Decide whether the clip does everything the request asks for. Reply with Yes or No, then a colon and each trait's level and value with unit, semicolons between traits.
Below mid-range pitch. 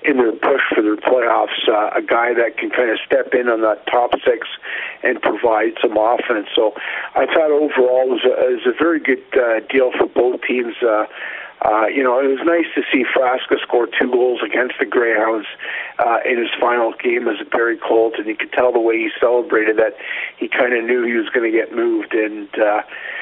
No: medium, 150 Hz